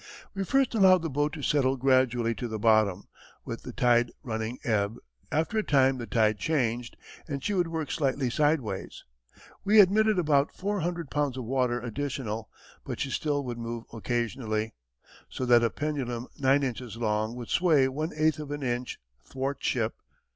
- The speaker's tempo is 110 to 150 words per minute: No, average, 170 wpm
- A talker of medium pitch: No, low, 130 Hz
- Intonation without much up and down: No, average, 4.4 semitones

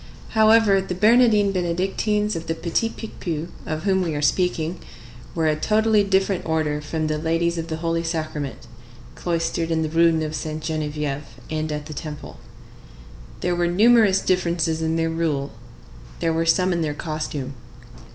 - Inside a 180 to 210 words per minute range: No, average, 160 wpm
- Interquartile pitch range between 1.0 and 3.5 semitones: Yes, average, 3.1 semitones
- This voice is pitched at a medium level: Yes, medium, 165 Hz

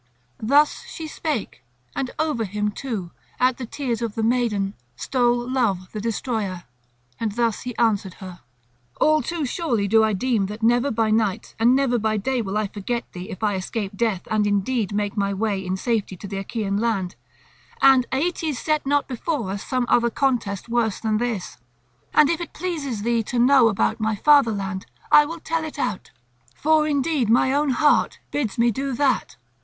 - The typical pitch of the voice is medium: No, high, 230 Hz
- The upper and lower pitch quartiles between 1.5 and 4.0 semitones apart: No, average, 4.6 semitones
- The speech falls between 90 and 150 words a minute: No, average, 185 wpm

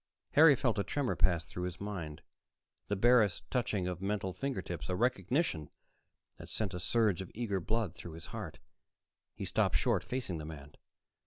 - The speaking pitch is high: No, very low, 95 Hz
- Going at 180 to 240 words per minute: No, average, 170 wpm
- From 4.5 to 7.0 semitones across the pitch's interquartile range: Yes, average, 5.1 semitones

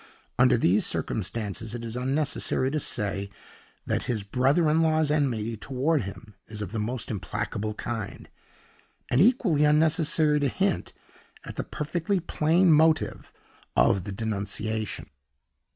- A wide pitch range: Yes, wide, 6.4 semitones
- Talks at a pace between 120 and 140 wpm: Yes, slow, 135 wpm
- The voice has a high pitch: No, low, 130 Hz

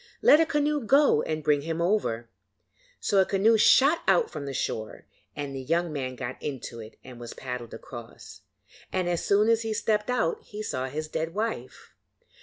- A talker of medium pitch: Yes, medium, 160 Hz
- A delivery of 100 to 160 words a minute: No, average, 190 wpm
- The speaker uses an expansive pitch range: Yes, wide, 8.9 semitones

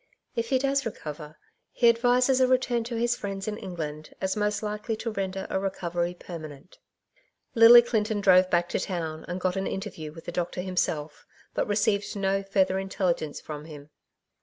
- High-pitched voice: Yes, high, 195 Hz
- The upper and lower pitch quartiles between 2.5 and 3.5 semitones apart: No, average, 4.4 semitones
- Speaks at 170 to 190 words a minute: Yes, average, 180 wpm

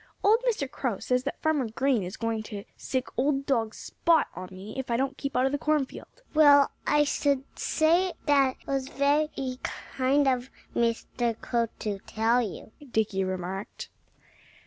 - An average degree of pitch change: Yes, average, 4.1 semitones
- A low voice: No, very high, 260 Hz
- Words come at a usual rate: Yes, average, 165 wpm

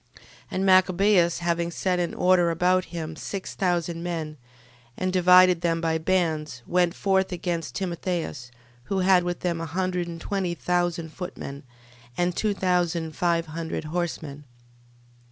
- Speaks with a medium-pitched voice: Yes, medium, 175 Hz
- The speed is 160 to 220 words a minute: No, average, 145 wpm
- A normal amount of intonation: No, narrow, 1.7 semitones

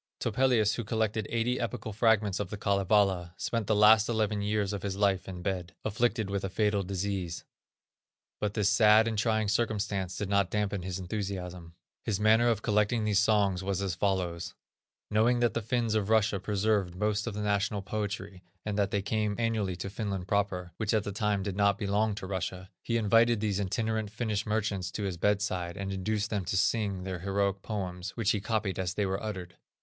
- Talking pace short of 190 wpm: No, average, 195 wpm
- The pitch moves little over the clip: Yes, narrow, 2.1 semitones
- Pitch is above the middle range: No, low, 100 Hz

